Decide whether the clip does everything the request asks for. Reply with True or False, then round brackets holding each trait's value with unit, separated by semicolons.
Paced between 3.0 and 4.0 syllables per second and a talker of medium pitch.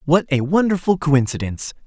False (5.6 syllables/s; 160 Hz)